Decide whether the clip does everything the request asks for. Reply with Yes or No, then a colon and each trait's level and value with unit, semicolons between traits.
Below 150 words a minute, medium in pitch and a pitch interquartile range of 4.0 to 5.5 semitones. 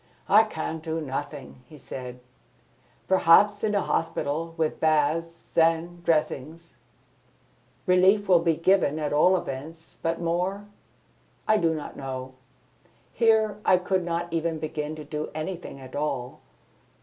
No: slow, 135 wpm; medium, 165 Hz; average, 3.1 semitones